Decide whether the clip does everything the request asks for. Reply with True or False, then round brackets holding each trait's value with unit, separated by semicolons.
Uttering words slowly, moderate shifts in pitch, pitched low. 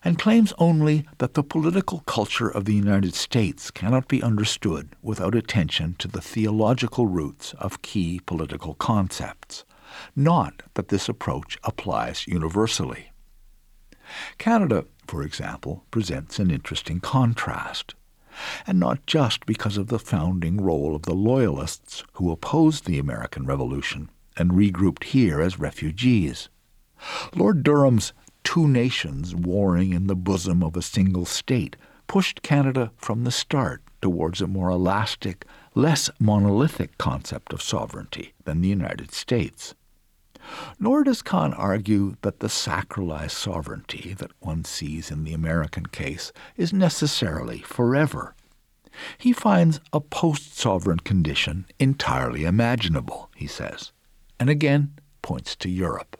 False (130 wpm; 7.3 semitones; 105 Hz)